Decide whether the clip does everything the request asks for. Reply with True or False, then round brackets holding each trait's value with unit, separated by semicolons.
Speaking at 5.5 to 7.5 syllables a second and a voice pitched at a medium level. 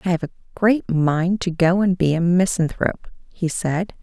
False (4.9 syllables/s; 175 Hz)